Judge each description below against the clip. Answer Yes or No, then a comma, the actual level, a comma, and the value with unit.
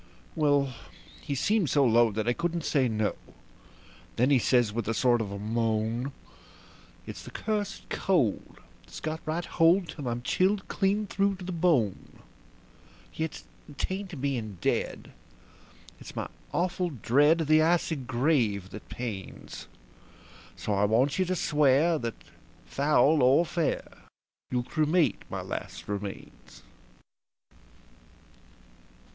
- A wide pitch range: Yes, wide, 6.4 semitones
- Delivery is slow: Yes, slow, 130 wpm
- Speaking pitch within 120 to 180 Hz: Yes, medium, 140 Hz